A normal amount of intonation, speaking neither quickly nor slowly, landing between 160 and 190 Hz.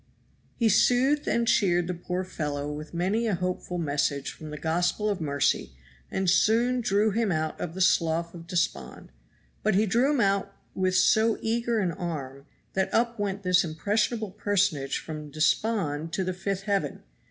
Yes: average, 4.9 semitones; average, 170 wpm; medium, 185 Hz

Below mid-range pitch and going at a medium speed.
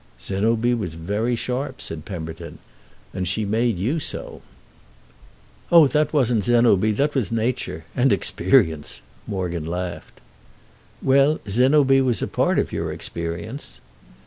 No: low, 110 Hz; slow, 125 wpm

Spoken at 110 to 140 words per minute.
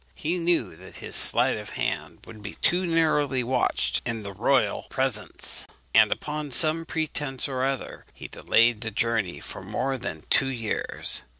No: average, 165 wpm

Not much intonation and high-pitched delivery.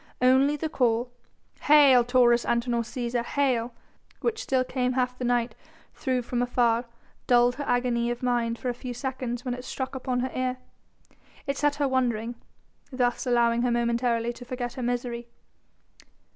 Yes: narrow, 1.3 semitones; high, 245 Hz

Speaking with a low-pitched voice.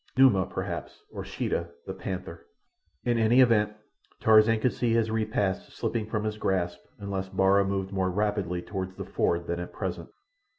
Yes: low, 100 Hz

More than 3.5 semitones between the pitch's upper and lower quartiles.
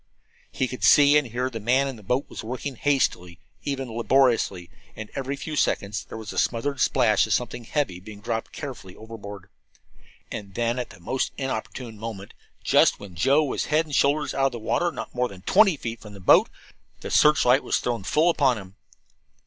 Yes: average, 4.6 semitones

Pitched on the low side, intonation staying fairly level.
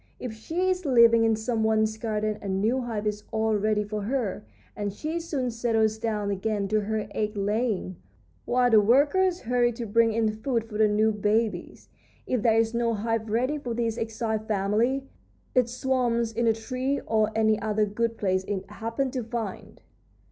No: high, 225 Hz; narrow, 2.1 semitones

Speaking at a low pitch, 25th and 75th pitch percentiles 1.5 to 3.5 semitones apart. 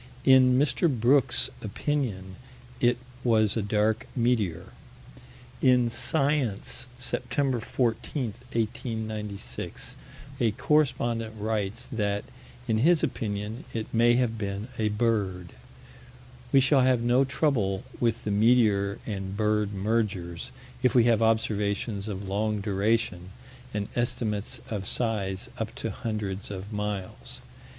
Yes: low, 110 Hz; average, 3.0 semitones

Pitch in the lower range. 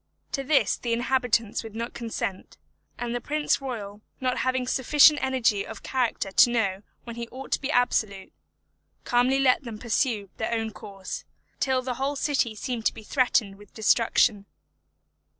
No: high, 240 Hz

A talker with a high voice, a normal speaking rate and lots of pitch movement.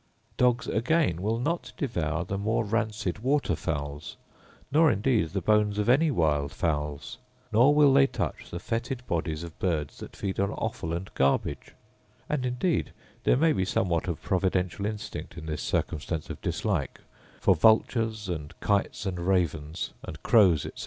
No: low, 100 Hz; average, 160 wpm; wide, 6.1 semitones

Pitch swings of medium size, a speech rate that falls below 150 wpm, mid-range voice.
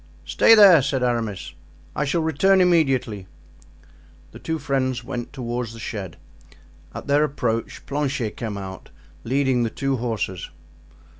No: average, 4.2 semitones; slow, 135 wpm; low, 130 Hz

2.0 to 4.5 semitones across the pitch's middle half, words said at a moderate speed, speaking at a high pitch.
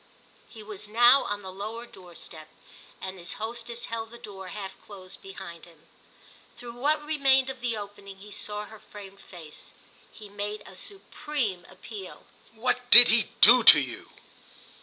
Yes: average, 3.8 semitones; average, 160 wpm; high, 210 Hz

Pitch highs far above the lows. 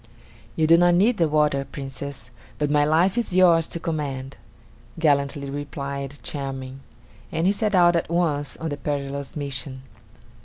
No: average, 3.3 semitones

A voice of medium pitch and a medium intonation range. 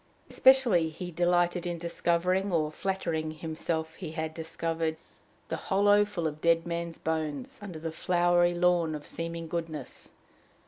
No: medium, 170 Hz; narrow, 1.8 semitones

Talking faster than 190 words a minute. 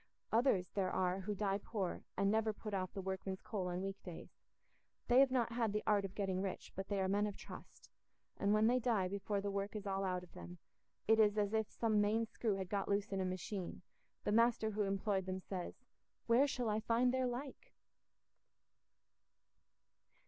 Yes: average, 200 wpm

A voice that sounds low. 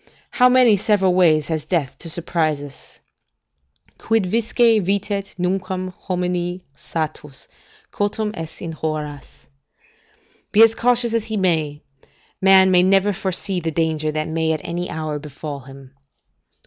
No: medium, 180 Hz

